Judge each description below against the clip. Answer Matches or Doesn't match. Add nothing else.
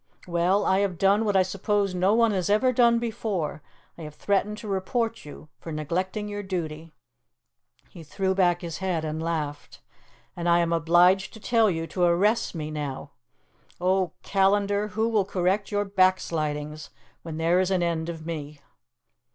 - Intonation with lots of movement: Doesn't match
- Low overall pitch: Doesn't match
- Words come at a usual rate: Matches